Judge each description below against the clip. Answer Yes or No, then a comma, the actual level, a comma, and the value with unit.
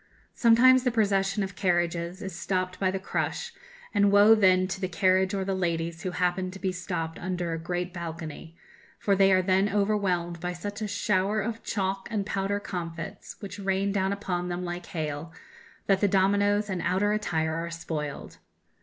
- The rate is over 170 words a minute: Yes, average, 180 wpm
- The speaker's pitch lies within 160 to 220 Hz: Yes, high, 190 Hz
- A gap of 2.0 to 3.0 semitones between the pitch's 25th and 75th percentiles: Yes, narrow, 2.4 semitones